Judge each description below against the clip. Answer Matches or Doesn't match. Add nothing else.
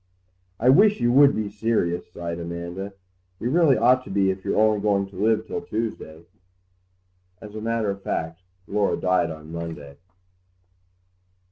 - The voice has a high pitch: Doesn't match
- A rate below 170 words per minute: Matches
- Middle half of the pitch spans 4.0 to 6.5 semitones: Matches